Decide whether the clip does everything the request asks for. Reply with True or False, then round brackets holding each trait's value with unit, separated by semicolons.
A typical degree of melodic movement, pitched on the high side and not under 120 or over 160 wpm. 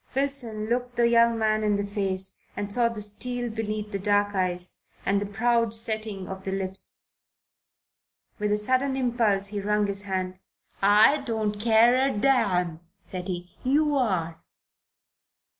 True (3.2 semitones; 210 Hz; 155 wpm)